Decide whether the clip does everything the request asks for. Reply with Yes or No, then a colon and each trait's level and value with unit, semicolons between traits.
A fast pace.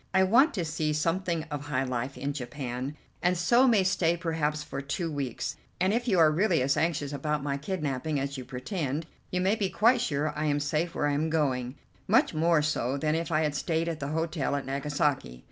Yes: fast, 215 wpm